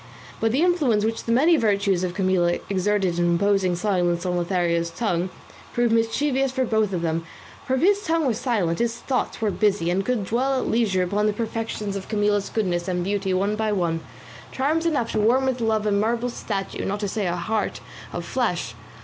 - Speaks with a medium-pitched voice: No, high, 210 Hz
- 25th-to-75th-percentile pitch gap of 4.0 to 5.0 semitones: Yes, average, 4.4 semitones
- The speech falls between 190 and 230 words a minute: Yes, average, 200 wpm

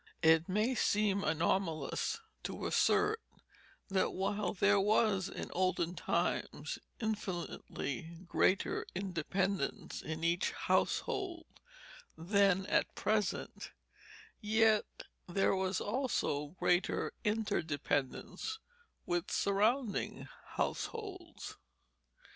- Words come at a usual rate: No, slow, 85 wpm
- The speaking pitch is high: Yes, high, 195 Hz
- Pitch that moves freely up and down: No, average, 3.5 semitones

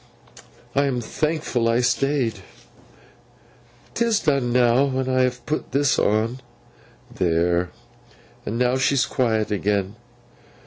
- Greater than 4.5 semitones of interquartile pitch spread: No, average, 3.9 semitones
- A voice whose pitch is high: No, low, 125 Hz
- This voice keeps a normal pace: No, slow, 115 wpm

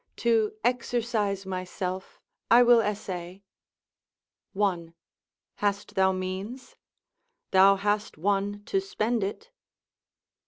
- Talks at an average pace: No, slow, 90 wpm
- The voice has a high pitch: Yes, high, 205 Hz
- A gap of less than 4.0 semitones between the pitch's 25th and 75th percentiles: Yes, average, 3.2 semitones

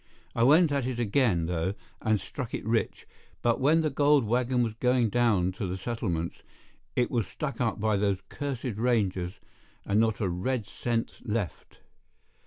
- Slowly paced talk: No, average, 170 wpm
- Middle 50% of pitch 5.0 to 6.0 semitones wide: No, average, 4.2 semitones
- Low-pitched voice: Yes, low, 115 Hz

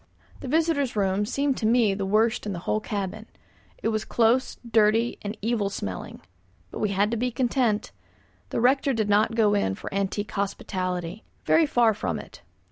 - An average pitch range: Yes, average, 3.0 semitones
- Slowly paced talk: No, average, 185 wpm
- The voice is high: Yes, high, 215 Hz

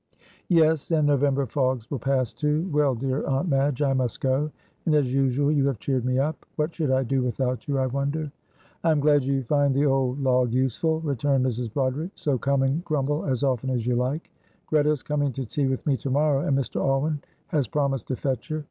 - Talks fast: Yes, fast, 220 wpm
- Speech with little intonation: Yes, narrow, 2.2 semitones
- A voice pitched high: No, low, 135 Hz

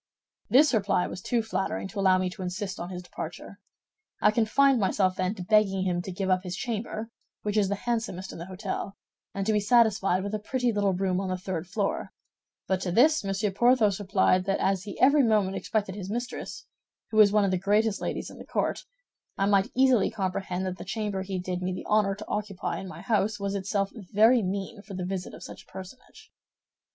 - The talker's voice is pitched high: Yes, high, 195 Hz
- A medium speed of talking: No, fast, 215 wpm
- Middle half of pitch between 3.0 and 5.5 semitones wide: No, narrow, 2.4 semitones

